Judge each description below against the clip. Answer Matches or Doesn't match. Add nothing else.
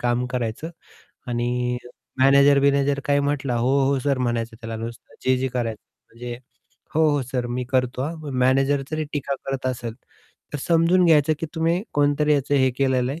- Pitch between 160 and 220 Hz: Doesn't match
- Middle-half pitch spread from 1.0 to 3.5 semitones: Matches